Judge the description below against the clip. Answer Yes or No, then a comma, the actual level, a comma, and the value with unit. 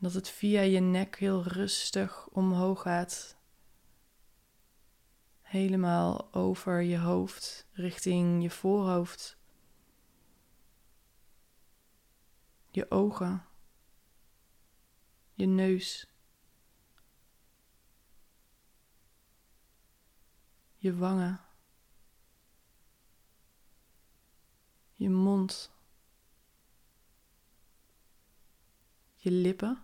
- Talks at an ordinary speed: No, slow, 50 wpm